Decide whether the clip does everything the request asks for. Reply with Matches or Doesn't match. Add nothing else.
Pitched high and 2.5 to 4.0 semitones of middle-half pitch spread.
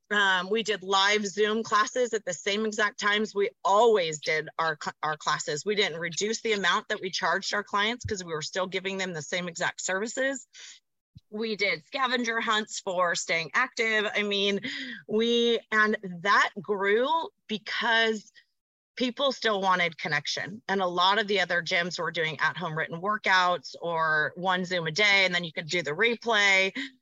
Matches